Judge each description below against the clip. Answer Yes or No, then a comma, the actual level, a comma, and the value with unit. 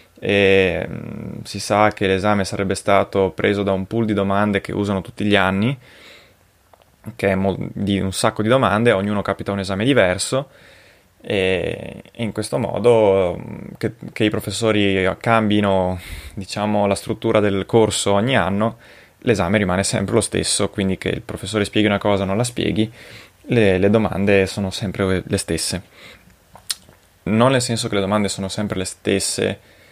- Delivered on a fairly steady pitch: Yes, narrow, 2.0 semitones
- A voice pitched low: Yes, low, 100 Hz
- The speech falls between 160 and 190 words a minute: Yes, average, 165 wpm